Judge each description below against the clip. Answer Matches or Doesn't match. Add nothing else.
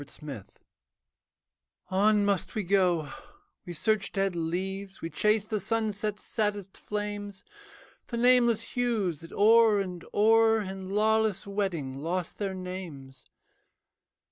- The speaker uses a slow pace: Matches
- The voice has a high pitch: Matches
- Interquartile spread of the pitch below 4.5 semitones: Matches